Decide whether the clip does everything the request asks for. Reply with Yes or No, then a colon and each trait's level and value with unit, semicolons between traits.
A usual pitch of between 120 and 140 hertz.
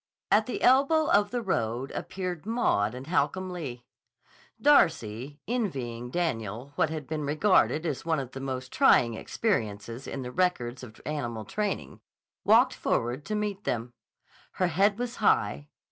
No: medium, 150 Hz